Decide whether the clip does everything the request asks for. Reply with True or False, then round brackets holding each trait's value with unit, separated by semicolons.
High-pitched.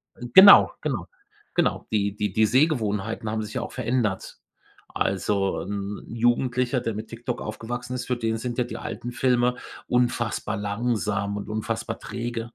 False (115 Hz)